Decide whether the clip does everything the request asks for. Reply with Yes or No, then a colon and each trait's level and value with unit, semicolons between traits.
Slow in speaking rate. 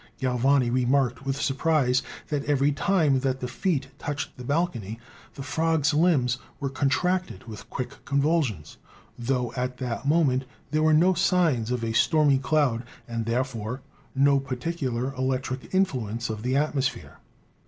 No: average, 150 wpm